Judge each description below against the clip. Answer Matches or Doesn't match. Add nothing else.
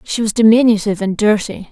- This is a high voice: Matches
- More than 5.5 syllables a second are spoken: Matches